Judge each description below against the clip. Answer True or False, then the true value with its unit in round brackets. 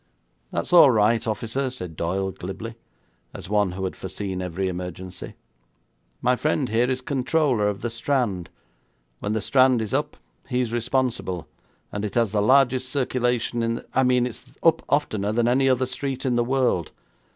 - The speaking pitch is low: True (120 Hz)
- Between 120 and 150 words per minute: False (175 wpm)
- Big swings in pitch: False (4.3 semitones)